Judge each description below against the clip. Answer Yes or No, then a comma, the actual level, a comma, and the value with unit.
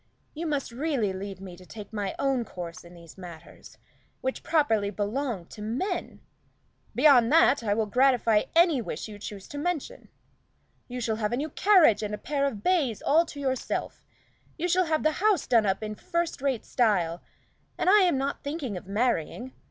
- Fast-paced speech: No, average, 185 wpm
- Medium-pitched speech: No, high, 245 Hz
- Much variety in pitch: Yes, wide, 6.5 semitones